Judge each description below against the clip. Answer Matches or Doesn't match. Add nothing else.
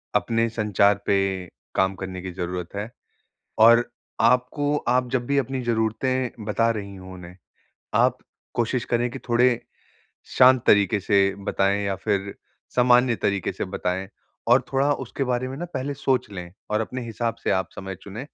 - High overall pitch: Doesn't match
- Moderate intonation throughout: Matches